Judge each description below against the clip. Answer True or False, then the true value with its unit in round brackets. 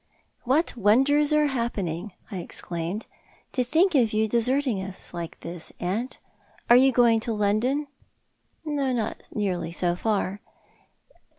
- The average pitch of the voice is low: False (225 Hz)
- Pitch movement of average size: False (5.7 semitones)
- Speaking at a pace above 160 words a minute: False (150 wpm)